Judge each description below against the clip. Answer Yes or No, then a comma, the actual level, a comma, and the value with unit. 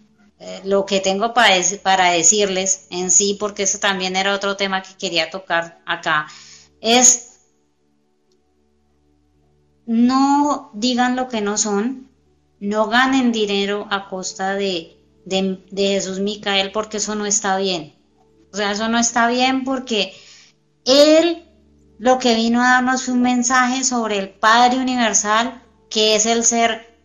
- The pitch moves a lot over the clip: No, average, 4.3 semitones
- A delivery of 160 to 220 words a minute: No, average, 145 wpm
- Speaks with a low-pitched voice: No, high, 200 Hz